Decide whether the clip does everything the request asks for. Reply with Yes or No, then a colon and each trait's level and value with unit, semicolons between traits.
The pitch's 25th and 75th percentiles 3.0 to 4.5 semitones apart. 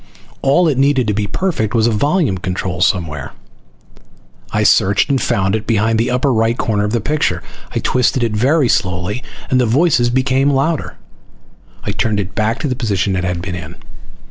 No: average, 5.1 semitones